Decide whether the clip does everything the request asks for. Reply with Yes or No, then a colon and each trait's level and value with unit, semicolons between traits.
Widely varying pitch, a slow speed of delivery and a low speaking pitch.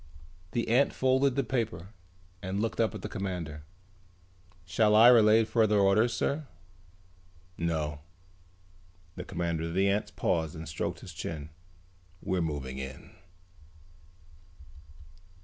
Yes: wide, 5.9 semitones; slow, 120 wpm; very low, 95 Hz